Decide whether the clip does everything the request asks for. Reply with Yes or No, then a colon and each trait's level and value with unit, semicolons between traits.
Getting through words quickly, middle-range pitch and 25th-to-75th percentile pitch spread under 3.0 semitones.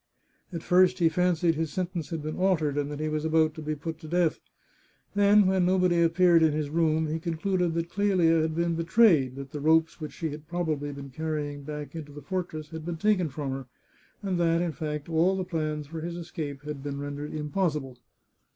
Yes: fast, 215 wpm; medium, 160 Hz; narrow, 2.6 semitones